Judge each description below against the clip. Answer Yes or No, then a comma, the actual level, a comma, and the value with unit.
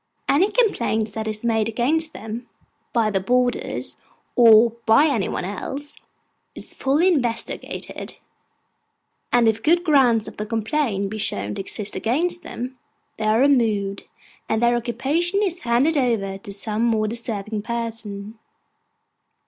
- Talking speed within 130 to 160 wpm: Yes, slow, 135 wpm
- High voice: Yes, high, 230 Hz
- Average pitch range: Yes, average, 4.0 semitones